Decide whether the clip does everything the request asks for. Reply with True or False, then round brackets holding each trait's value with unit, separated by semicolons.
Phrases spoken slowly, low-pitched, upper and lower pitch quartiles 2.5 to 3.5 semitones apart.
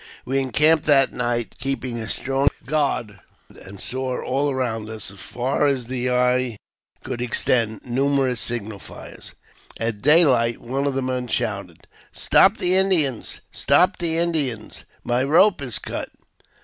False (150 wpm; 130 Hz; 3.2 semitones)